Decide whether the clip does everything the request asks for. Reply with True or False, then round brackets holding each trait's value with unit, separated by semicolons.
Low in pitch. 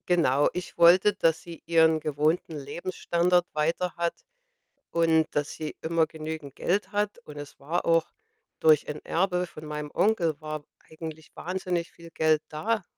False (165 Hz)